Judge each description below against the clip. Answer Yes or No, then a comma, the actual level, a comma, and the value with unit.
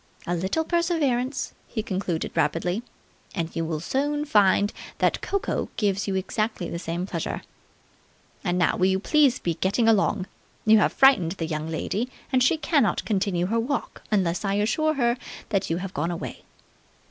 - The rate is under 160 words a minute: No, average, 170 wpm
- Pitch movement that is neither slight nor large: No, wide, 6.1 semitones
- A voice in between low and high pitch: No, high, 200 Hz